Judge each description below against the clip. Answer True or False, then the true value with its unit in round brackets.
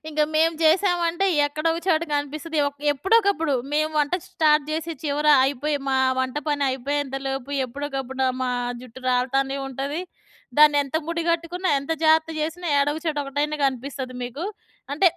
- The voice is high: True (295 Hz)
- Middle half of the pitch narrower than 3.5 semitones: True (3.1 semitones)